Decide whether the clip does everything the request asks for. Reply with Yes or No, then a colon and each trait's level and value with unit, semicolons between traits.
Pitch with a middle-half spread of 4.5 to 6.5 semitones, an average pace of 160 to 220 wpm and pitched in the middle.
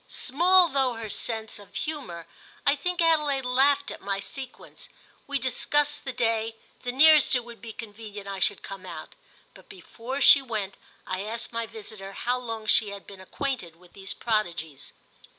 No: average, 5.3 semitones; average, 170 wpm; high, 230 Hz